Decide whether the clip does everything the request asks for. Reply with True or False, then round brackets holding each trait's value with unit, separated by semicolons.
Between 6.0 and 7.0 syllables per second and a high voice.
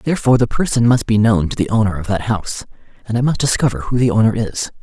False (6.7 syllables/s; 110 Hz)